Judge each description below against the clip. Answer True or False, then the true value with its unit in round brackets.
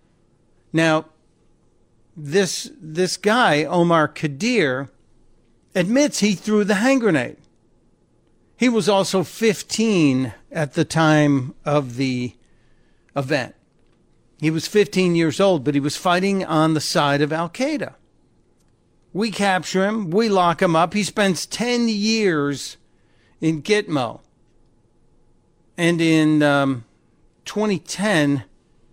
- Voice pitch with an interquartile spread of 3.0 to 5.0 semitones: False (5.6 semitones)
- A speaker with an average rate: False (110 wpm)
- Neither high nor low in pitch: True (165 Hz)